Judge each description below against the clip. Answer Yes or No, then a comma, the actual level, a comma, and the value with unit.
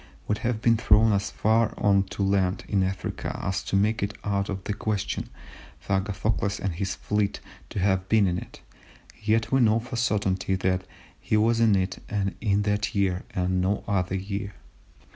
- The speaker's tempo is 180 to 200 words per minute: Yes, average, 185 wpm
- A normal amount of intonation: No, narrow, 2.1 semitones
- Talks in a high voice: No, low, 100 Hz